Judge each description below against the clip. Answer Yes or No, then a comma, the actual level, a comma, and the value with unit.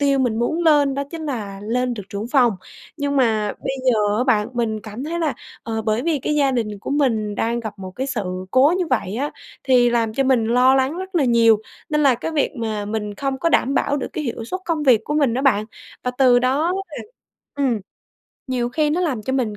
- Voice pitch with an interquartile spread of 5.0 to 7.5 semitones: No, average, 4.2 semitones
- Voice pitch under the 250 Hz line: No, very high, 255 Hz